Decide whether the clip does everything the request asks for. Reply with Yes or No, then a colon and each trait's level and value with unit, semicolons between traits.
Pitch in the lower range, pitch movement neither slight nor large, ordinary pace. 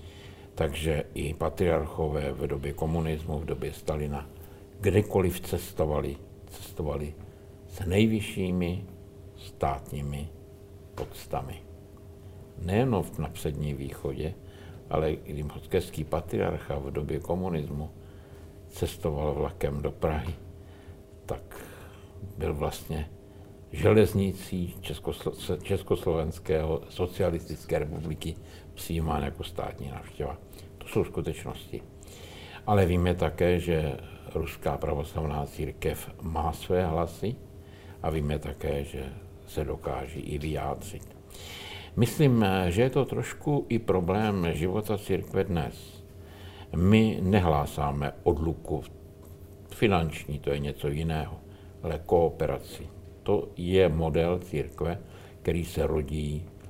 No: very low, 85 Hz; average, 4.2 semitones; slow, 95 wpm